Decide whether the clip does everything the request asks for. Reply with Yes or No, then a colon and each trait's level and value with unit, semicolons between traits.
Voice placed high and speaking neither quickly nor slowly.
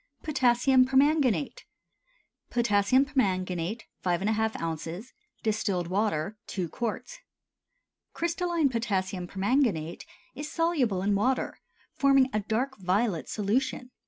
No: high, 220 Hz; slow, 95 wpm